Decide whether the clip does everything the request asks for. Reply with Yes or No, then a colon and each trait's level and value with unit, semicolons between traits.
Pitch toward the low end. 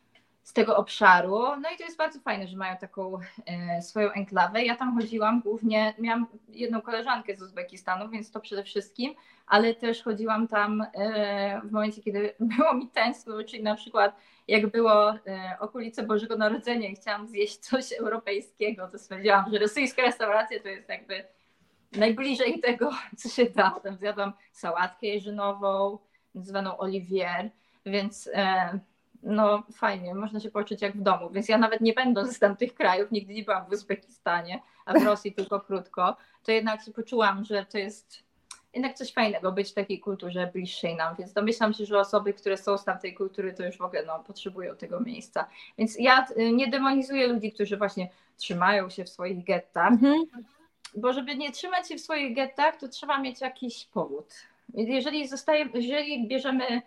No: high, 215 Hz